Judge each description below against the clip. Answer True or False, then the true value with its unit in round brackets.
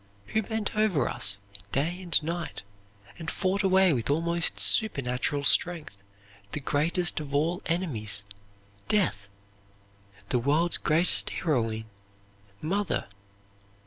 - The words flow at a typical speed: False (110 wpm)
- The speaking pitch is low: False (160 Hz)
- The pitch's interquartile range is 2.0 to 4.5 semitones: False (5.0 semitones)